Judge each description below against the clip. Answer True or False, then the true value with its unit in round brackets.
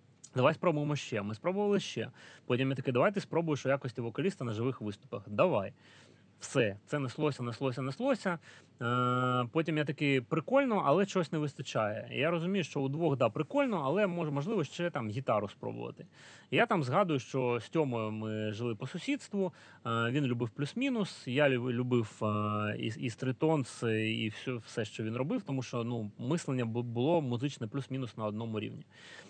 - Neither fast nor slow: False (160 wpm)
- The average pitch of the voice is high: False (130 Hz)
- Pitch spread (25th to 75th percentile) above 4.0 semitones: True (5.1 semitones)